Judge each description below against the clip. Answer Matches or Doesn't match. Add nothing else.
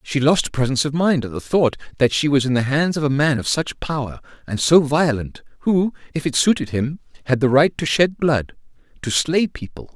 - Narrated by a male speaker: Matches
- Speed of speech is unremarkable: Doesn't match